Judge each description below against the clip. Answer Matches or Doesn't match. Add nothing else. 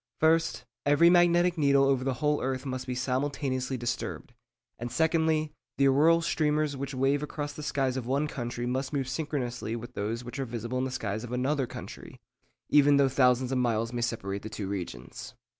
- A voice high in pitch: Doesn't match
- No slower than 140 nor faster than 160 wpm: Doesn't match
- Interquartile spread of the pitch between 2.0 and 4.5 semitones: Matches